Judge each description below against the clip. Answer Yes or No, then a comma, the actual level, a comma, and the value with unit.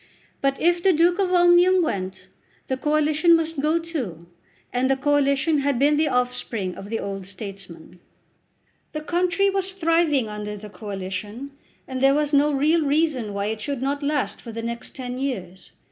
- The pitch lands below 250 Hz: No, very high, 275 Hz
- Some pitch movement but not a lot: No, wide, 6.7 semitones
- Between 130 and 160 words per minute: No, average, 175 wpm